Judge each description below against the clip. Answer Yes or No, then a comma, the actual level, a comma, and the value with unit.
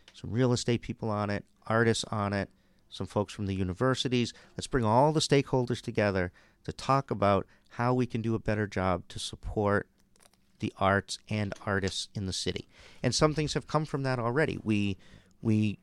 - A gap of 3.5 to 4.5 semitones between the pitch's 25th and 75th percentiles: Yes, average, 4.0 semitones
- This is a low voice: Yes, low, 110 Hz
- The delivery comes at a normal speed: Yes, average, 185 wpm